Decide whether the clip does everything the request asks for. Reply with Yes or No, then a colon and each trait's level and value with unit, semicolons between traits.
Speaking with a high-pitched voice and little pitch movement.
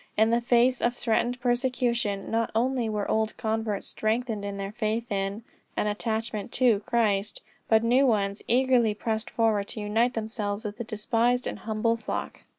Yes: high, 225 Hz; narrow, 2.2 semitones